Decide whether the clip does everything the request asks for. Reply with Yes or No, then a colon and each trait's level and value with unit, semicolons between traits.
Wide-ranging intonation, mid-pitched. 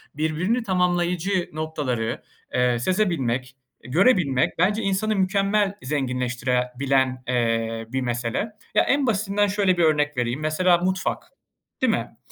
Yes: wide, 7.2 semitones; medium, 155 Hz